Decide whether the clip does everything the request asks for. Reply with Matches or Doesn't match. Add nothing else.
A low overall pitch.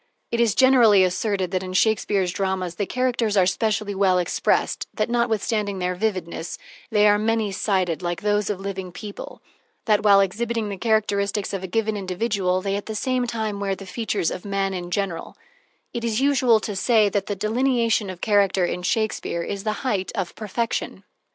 Doesn't match